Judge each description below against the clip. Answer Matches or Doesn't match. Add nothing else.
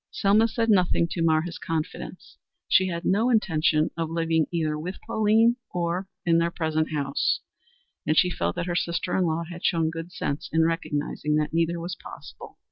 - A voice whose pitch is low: Doesn't match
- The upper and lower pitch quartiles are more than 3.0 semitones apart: Doesn't match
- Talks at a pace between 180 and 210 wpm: Matches